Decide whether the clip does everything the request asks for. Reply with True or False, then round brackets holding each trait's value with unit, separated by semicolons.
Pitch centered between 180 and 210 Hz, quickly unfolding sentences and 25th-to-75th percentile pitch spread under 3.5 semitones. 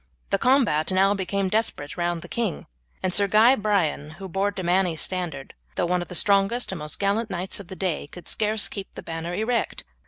True (190 Hz; 210 wpm; 3.1 semitones)